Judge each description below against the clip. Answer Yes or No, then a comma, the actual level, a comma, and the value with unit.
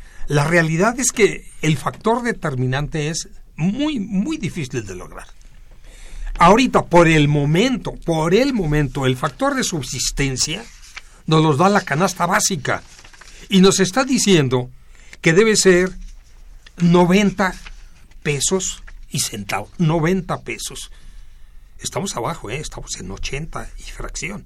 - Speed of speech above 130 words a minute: No, slow, 125 wpm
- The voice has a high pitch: No, medium, 165 Hz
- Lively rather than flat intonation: Yes, wide, 5.7 semitones